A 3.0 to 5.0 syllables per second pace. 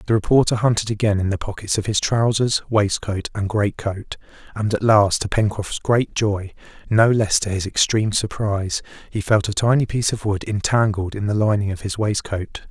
No: 5.2 syllables/s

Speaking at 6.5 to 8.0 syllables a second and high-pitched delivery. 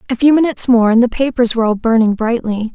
Yes: 6.7 syllables/s; high, 235 Hz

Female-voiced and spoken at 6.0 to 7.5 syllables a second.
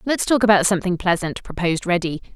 Yes: female; 6.6 syllables/s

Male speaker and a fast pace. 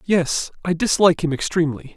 No: male; average, 155 wpm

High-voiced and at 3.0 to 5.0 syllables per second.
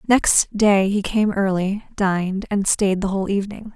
Yes: high, 200 Hz; 4.7 syllables/s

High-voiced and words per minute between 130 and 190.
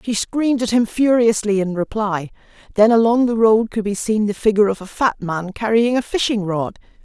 No: high, 215 Hz; fast, 205 wpm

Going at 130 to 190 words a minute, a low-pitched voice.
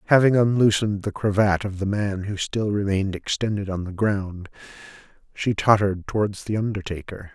Yes: average, 155 wpm; low, 100 Hz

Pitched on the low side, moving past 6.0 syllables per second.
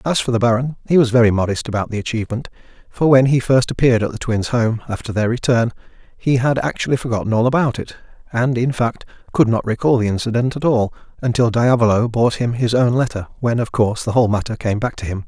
Yes: low, 120 Hz; 6.3 syllables/s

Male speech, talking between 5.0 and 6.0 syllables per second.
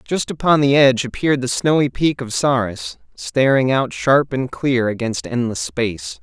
No: male; 4.7 syllables/s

